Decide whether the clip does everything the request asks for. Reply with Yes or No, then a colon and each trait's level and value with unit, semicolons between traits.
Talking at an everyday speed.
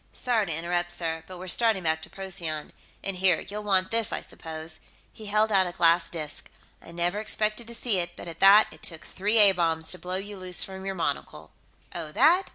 No: fast, 220 wpm